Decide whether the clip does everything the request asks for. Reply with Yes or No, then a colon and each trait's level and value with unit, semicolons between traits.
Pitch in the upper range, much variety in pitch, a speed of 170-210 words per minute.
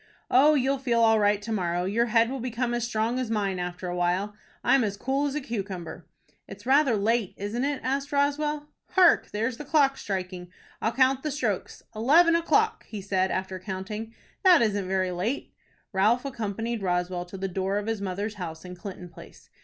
Yes: high, 220 Hz; wide, 5.7 semitones; average, 195 wpm